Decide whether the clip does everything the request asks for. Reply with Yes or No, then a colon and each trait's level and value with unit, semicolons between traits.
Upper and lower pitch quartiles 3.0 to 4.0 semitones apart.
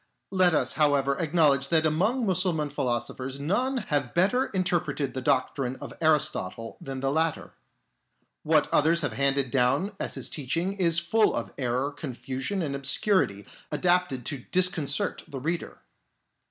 No: average, 4.6 semitones